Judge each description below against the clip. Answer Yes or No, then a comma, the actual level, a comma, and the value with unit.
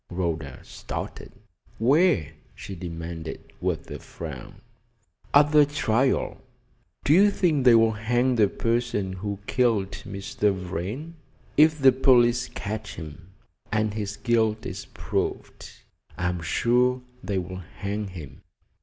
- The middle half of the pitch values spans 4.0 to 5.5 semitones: Yes, average, 5.2 semitones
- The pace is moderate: No, slow, 125 wpm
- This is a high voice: No, low, 110 Hz